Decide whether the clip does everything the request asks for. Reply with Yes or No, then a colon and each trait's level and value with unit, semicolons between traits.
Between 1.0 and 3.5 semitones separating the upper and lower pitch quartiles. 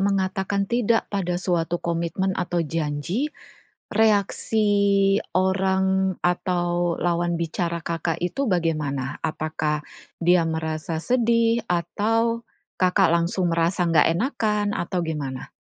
Yes: average, 3.0 semitones